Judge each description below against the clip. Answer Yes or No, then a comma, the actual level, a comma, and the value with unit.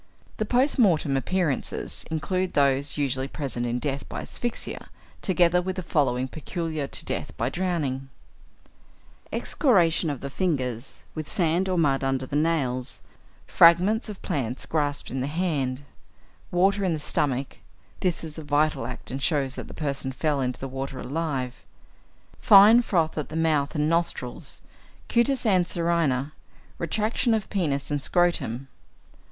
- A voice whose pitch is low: No, medium, 155 Hz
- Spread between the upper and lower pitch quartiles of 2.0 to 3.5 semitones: No, average, 4.7 semitones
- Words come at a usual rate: Yes, average, 145 wpm